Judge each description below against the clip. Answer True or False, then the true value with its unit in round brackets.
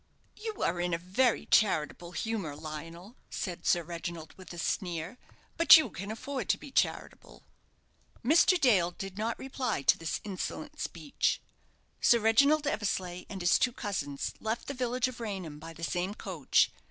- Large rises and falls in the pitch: True (6.0 semitones)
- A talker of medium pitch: False (195 Hz)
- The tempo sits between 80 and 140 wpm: False (165 wpm)